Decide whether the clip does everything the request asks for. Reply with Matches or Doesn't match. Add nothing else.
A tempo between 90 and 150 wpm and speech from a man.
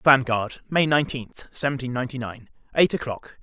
Matches